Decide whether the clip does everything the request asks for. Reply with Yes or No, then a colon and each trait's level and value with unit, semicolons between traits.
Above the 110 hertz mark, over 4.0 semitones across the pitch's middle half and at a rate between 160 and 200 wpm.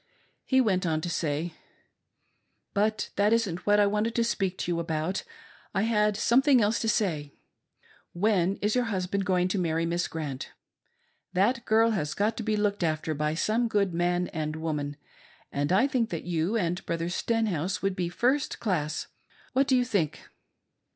Yes: high, 190 Hz; average, 4.7 semitones; average, 180 wpm